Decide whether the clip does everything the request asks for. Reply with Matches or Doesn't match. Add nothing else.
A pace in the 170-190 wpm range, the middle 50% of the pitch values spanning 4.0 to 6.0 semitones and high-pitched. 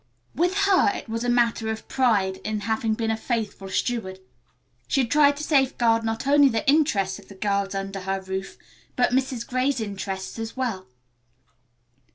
Matches